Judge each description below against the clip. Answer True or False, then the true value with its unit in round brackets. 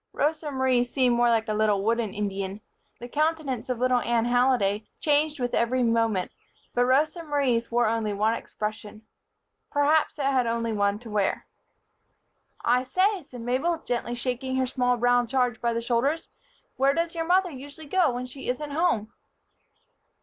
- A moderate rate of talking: True (165 wpm)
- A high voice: True (245 Hz)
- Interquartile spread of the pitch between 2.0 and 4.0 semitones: True (3.7 semitones)